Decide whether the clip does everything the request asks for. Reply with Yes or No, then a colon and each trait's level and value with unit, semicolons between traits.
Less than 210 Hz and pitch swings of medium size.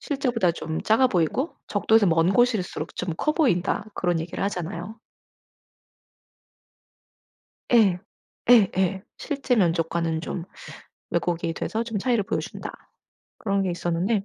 Yes: high, 190 Hz; average, 4.8 semitones